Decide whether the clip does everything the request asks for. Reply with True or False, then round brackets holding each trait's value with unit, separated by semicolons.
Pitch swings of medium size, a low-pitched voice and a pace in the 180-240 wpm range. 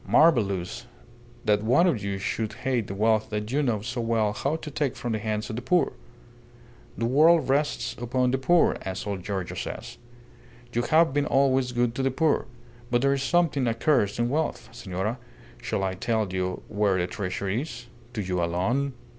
True (4.8 semitones; 120 Hz; 190 wpm)